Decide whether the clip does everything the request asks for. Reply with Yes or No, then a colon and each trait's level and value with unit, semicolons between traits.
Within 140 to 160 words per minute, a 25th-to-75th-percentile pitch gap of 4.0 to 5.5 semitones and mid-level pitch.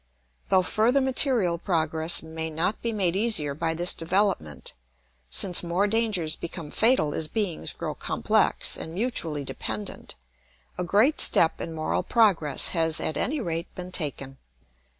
Yes: average, 145 wpm; average, 4.8 semitones; medium, 170 Hz